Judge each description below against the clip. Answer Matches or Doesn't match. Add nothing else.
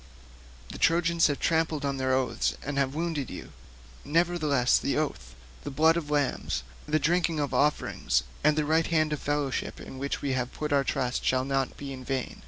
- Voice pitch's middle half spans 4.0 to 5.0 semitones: Doesn't match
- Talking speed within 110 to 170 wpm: Doesn't match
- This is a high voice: Doesn't match